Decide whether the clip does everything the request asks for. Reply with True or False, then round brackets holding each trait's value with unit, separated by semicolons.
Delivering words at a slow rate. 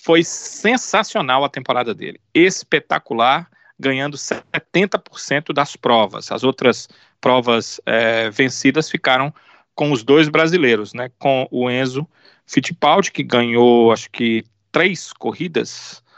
True (115 wpm)